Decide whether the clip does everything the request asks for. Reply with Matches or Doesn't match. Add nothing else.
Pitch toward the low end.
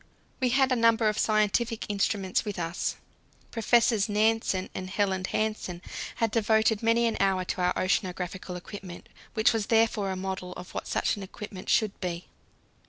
Doesn't match